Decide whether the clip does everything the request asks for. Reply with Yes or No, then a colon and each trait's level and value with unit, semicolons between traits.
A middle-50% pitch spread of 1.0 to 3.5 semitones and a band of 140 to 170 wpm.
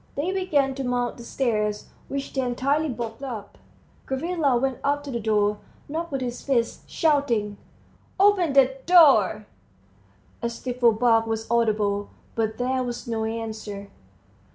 No: average, 3.9 semitones; average, 145 wpm